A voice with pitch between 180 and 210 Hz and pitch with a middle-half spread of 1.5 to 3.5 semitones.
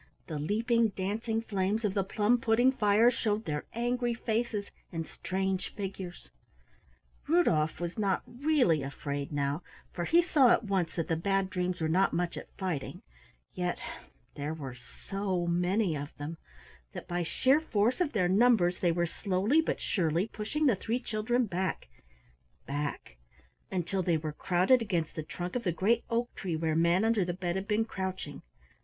No: high, 190 Hz; average, 4.9 semitones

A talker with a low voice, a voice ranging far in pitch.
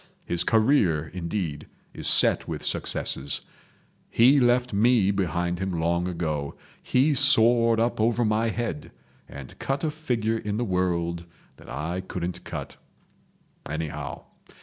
Yes: low, 100 Hz; wide, 5.7 semitones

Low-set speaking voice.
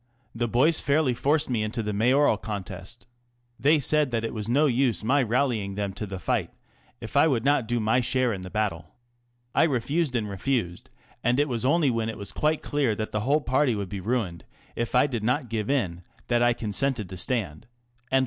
Yes: low, 120 Hz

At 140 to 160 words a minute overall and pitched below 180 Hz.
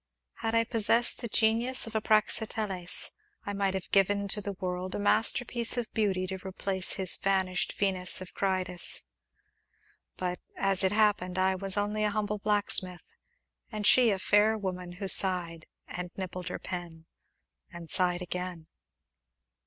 No: average, 155 wpm; high, 195 Hz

